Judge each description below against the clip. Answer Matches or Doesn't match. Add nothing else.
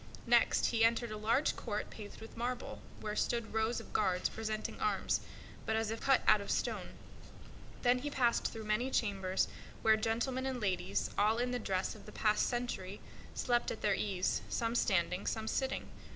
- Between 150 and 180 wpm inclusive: Doesn't match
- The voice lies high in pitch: Matches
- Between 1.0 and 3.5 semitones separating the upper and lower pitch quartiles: Matches